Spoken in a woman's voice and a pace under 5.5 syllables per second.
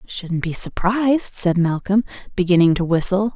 Yes: female; 4.8 syllables/s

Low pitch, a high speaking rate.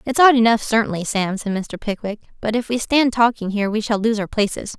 No: high, 220 Hz; fast, 240 wpm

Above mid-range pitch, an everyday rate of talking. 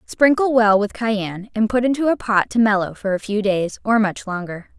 No: high, 215 Hz; fast, 225 wpm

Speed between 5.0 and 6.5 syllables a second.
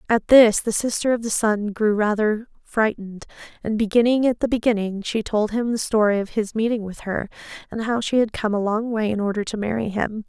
Yes: 5.5 syllables/s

